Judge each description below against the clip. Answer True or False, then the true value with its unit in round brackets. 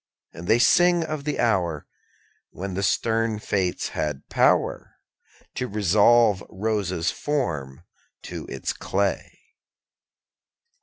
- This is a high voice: False (100 Hz)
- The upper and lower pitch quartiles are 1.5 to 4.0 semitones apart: False (4.8 semitones)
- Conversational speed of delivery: False (105 wpm)